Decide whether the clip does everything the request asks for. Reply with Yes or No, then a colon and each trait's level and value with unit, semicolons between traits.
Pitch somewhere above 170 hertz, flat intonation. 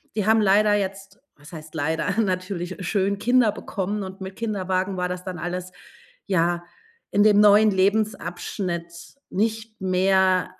Yes: high, 190 Hz; narrow, 2.3 semitones